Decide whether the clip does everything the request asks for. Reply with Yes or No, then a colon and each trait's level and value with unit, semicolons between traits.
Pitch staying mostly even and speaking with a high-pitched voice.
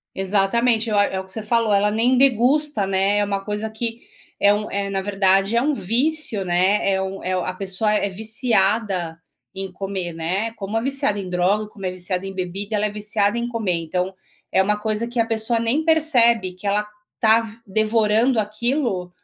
No: average, 3.1 semitones; high, 210 Hz